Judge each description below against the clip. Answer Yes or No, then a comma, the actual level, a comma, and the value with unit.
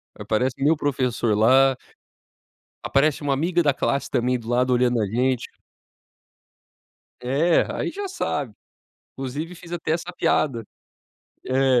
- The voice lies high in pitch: No, low, 135 Hz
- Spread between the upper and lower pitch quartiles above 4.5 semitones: No, average, 3.8 semitones